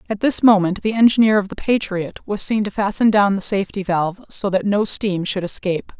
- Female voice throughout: Yes, female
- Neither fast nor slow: No, fast, 220 wpm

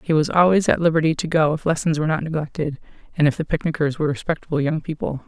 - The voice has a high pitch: No, medium, 155 Hz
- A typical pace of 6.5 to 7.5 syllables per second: Yes, 7.1 syllables/s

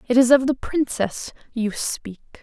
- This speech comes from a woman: Yes, female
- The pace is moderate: Yes, average, 175 wpm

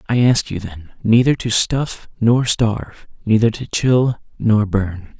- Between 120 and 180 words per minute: Yes, average, 160 wpm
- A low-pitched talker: Yes, low, 110 Hz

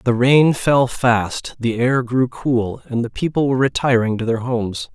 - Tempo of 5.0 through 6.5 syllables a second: No, 4.4 syllables/s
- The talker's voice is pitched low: Yes, low, 125 Hz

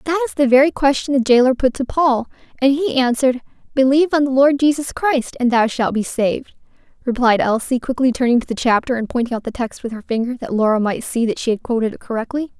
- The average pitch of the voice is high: Yes, very high, 255 Hz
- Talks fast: Yes, fast, 235 wpm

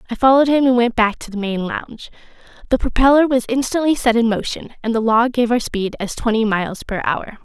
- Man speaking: No, female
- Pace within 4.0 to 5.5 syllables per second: No, 5.9 syllables/s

